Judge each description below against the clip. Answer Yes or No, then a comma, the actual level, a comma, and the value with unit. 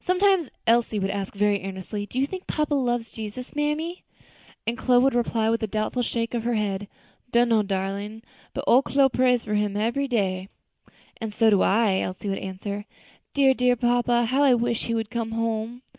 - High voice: Yes, high, 230 Hz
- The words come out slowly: No, average, 190 wpm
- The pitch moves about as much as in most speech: Yes, average, 3.2 semitones